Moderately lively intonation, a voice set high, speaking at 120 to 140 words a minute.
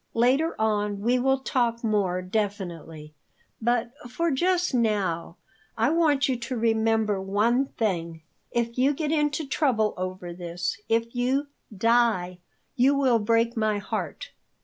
Yes: average, 4.4 semitones; high, 230 Hz; slow, 135 wpm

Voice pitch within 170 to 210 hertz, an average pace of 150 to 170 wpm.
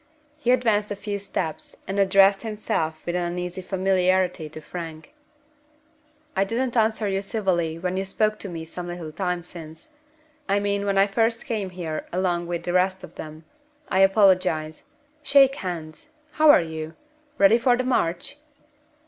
Yes: high, 190 Hz; average, 165 wpm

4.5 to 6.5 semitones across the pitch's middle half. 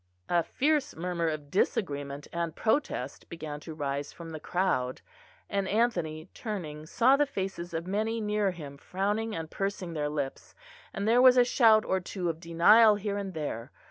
Yes: average, 5.3 semitones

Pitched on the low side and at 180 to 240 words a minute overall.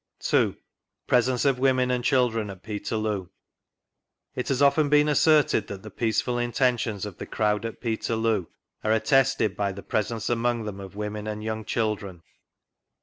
No: low, 110 Hz; average, 160 wpm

